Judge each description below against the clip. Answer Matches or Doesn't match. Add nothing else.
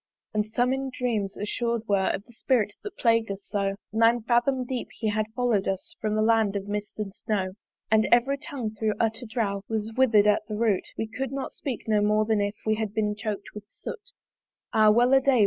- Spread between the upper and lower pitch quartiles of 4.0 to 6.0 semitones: Doesn't match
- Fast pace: Matches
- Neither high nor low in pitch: Doesn't match